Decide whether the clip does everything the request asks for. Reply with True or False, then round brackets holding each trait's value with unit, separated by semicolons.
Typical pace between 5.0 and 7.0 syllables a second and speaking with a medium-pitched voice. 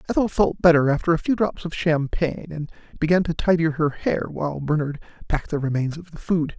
True (5.9 syllables/s; 160 Hz)